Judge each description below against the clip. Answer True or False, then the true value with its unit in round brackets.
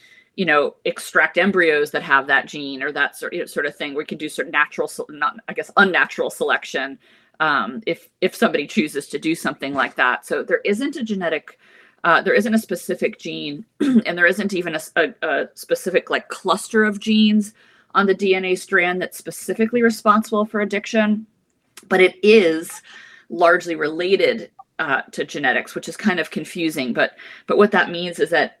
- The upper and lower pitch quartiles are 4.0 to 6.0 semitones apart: True (5.1 semitones)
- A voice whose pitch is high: True (200 Hz)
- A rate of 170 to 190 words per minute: True (185 wpm)